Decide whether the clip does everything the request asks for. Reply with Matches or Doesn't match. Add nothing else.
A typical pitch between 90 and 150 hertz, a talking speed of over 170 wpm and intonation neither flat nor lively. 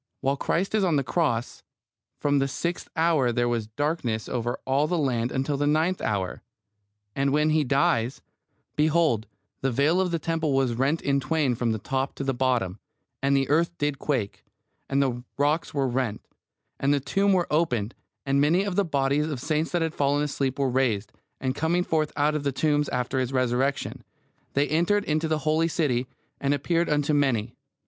Matches